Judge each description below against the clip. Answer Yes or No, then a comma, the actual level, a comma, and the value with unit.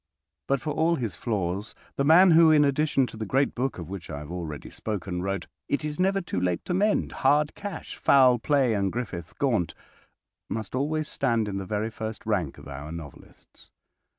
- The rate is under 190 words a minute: No, average, 195 wpm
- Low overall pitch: Yes, low, 115 Hz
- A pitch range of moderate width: No, wide, 8.0 semitones